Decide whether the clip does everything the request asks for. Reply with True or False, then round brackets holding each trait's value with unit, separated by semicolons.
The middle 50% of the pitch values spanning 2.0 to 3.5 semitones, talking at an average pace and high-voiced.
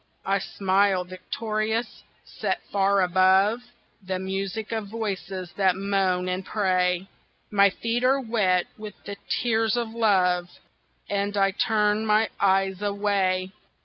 False (2.4 semitones; 125 wpm; 200 Hz)